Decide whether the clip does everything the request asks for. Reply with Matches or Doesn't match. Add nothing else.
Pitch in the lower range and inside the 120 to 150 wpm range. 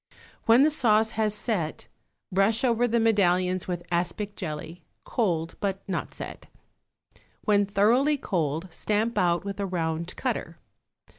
Doesn't match